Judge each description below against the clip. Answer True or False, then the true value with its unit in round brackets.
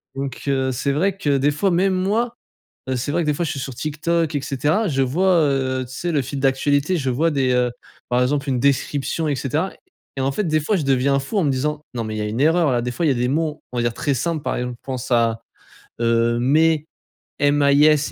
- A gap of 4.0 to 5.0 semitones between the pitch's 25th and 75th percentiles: False (3.4 semitones)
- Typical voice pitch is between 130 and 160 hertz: True (140 Hz)